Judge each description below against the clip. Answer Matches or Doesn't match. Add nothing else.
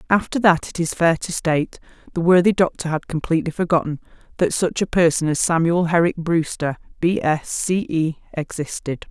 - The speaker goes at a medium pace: Matches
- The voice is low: Doesn't match